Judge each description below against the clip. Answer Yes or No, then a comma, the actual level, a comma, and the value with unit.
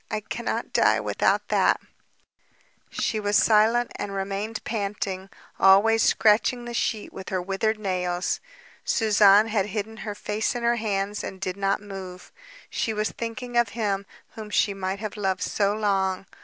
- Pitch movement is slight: Yes, narrow, 2.1 semitones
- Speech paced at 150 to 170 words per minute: Yes, average, 155 wpm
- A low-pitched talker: No, high, 205 Hz